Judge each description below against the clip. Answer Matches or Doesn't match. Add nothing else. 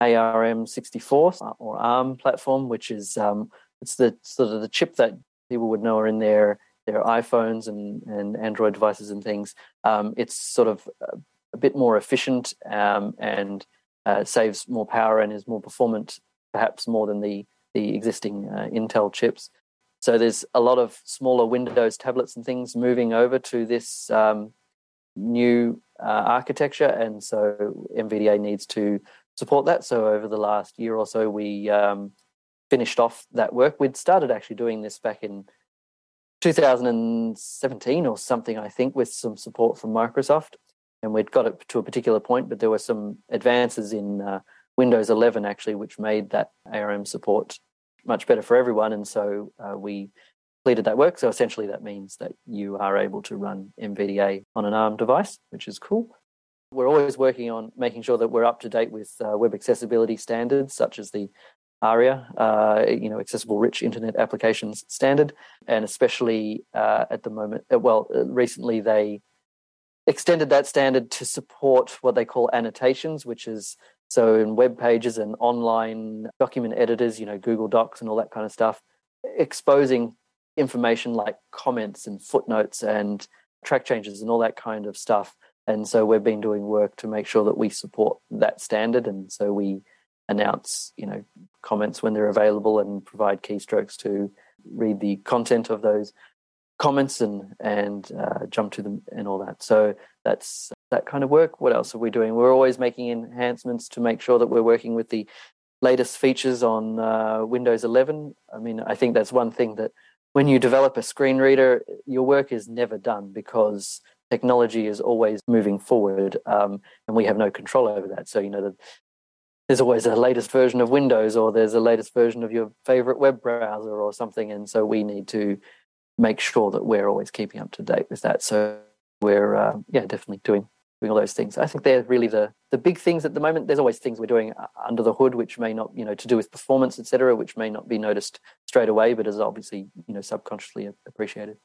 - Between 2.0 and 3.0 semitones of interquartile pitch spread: Matches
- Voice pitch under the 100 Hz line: Doesn't match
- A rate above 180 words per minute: Matches